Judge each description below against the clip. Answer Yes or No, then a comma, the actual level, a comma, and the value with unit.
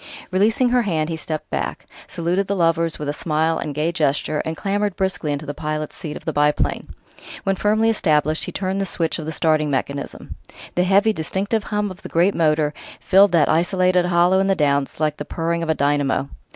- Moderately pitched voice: Yes, medium, 165 Hz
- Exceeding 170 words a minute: Yes, fast, 205 wpm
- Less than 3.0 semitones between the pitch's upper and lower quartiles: No, average, 4.0 semitones